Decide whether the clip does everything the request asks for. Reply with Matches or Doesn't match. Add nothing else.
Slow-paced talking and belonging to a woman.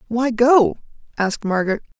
Matches